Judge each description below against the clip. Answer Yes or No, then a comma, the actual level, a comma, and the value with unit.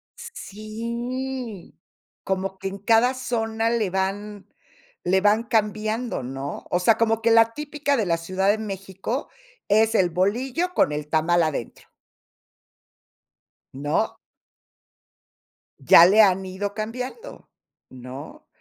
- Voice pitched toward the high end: Yes, high, 210 Hz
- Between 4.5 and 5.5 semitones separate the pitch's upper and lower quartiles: No, average, 3.6 semitones